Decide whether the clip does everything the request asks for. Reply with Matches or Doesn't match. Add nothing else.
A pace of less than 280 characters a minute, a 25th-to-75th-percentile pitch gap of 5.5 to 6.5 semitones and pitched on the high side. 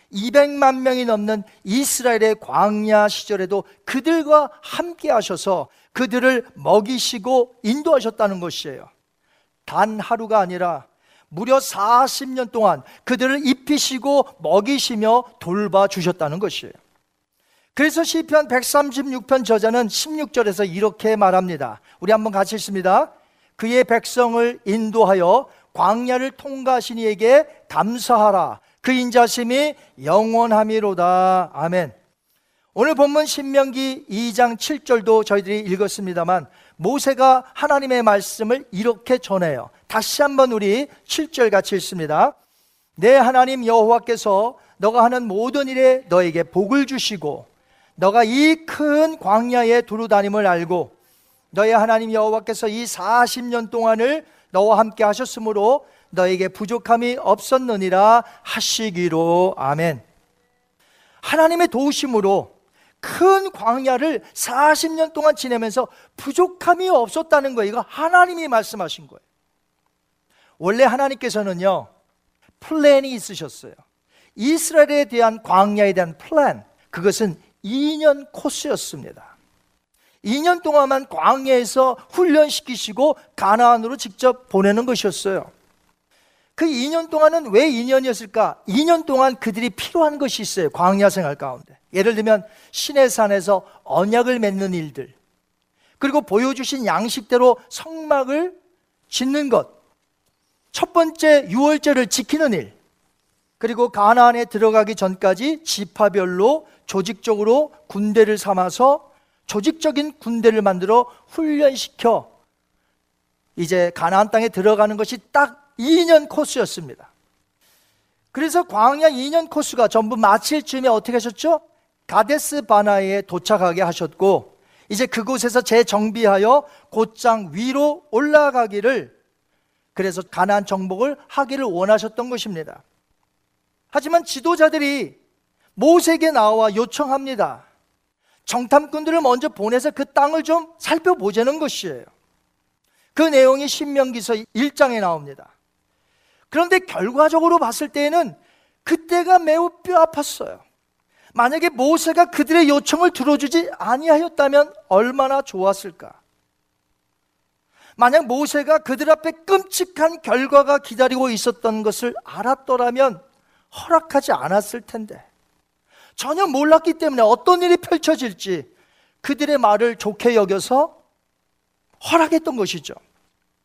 Matches